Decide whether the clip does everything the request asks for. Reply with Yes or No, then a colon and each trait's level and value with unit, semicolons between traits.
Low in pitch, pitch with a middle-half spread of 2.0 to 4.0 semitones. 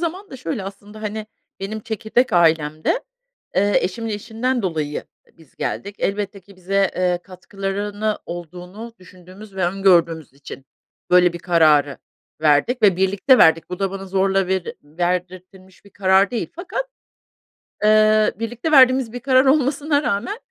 No: high, 195 Hz; average, 3.7 semitones